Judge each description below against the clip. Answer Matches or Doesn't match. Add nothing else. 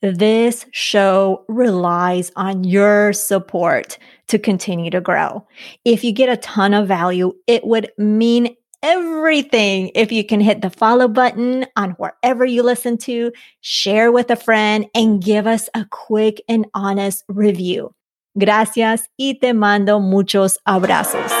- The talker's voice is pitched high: Matches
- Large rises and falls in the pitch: Doesn't match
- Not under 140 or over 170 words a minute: Matches